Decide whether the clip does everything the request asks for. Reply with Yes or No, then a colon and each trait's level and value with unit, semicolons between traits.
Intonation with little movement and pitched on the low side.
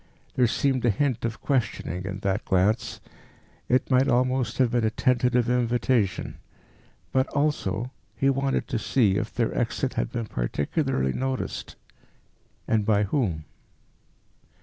No: average, 4.3 semitones; low, 120 Hz